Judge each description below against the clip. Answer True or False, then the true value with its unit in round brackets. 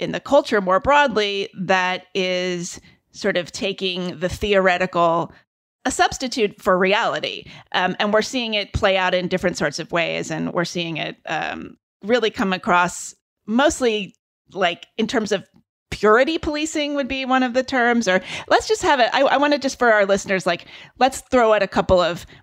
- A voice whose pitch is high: True (205 Hz)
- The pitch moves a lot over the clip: True (5.8 semitones)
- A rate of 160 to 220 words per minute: True (185 wpm)